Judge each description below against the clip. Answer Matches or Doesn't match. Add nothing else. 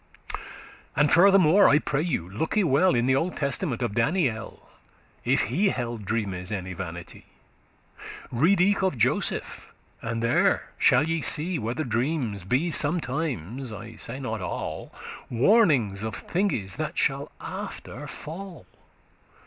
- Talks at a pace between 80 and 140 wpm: Matches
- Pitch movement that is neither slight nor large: Doesn't match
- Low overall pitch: Matches